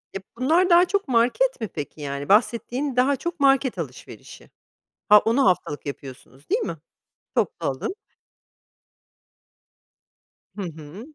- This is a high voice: Yes, high, 235 Hz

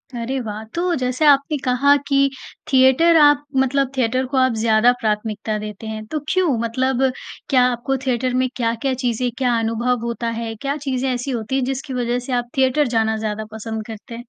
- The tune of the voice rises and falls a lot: No, average, 2.8 semitones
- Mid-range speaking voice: No, very high, 250 Hz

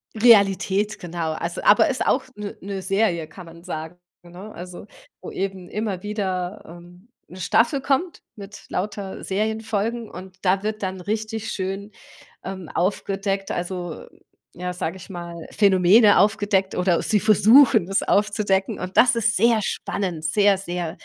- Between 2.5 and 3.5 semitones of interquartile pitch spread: Yes, average, 2.9 semitones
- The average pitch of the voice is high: Yes, high, 195 Hz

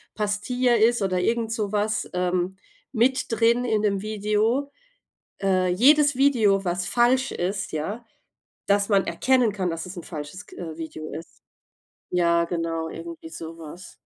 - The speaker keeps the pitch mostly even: No, average, 4.7 semitones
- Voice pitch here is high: Yes, high, 200 Hz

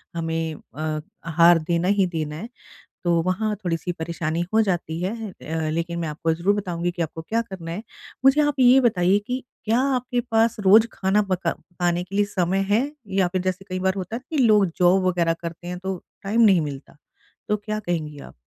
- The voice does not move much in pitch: No, average, 3.8 semitones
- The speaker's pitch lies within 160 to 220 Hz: Yes, medium, 185 Hz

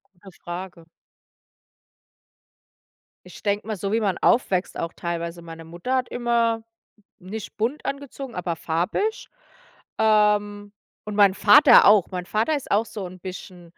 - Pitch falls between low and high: No, high, 205 Hz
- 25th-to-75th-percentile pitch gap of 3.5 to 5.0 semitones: Yes, average, 3.9 semitones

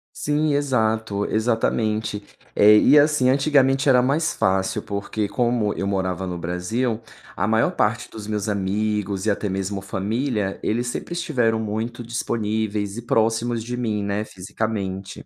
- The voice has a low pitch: Yes, low, 110 Hz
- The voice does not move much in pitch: No, average, 3.2 semitones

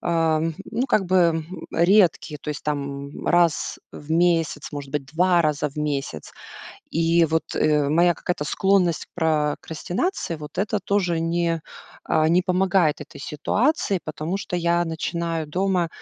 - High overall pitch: No, medium, 165 Hz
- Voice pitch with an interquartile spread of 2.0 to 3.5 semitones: Yes, average, 2.8 semitones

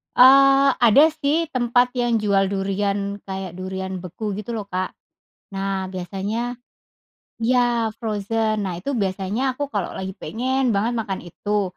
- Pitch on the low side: No, high, 210 Hz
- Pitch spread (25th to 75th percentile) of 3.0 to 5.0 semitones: Yes, average, 4.0 semitones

